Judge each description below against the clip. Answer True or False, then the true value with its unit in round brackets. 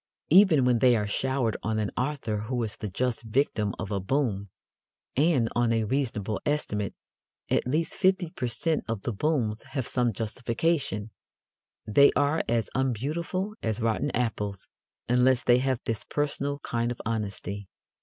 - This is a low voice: True (120 Hz)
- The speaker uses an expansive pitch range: False (4.6 semitones)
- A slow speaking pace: False (155 wpm)